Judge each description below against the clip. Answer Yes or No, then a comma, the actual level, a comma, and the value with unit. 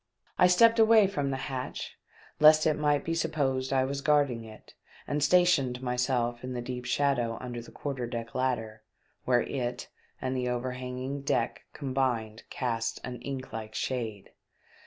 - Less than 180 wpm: Yes, average, 155 wpm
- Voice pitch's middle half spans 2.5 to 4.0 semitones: Yes, average, 2.8 semitones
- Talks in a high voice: No, low, 130 Hz